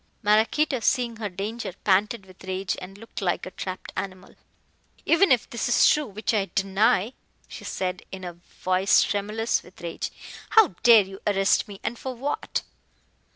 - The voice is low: No, high, 205 Hz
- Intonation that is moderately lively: Yes, average, 3.5 semitones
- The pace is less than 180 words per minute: Yes, average, 165 wpm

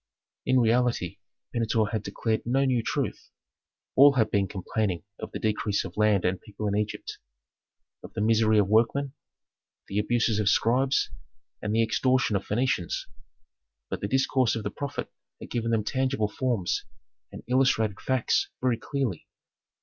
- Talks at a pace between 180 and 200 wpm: No, average, 155 wpm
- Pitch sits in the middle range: No, low, 115 Hz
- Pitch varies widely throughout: No, average, 3.3 semitones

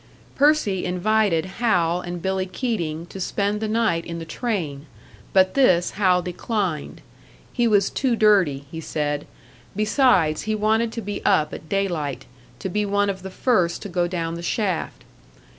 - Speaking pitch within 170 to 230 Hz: Yes, high, 190 Hz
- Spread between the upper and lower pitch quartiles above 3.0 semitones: Yes, average, 4.2 semitones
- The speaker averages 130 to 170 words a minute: Yes, average, 160 wpm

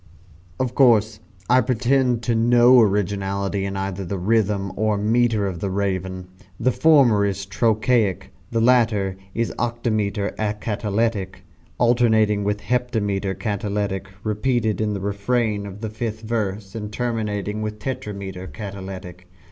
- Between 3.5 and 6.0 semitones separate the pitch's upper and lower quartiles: No, average, 2.8 semitones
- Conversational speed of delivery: No, slow, 130 wpm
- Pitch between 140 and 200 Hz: No, low, 105 Hz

